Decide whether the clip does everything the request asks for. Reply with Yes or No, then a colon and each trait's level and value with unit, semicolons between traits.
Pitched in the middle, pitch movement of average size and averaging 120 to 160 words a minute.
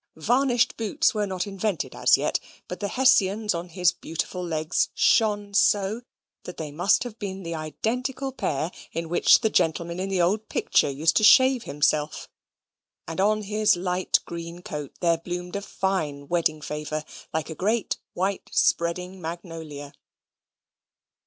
Yes: medium, 180 Hz; average, 4.3 semitones; average, 150 wpm